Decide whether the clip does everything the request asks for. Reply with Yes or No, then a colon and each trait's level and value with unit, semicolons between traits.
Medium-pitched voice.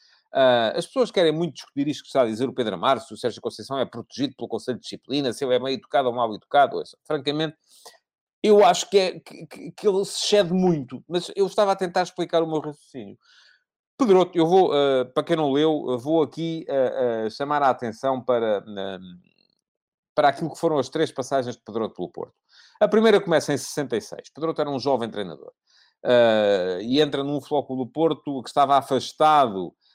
Yes: medium, 145 Hz